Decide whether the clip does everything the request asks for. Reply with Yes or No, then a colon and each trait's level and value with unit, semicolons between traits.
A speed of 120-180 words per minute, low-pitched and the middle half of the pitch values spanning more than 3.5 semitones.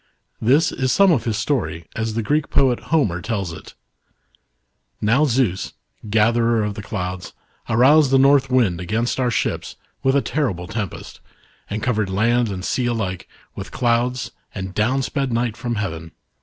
Yes: average, 170 wpm; low, 115 Hz; average, 4.4 semitones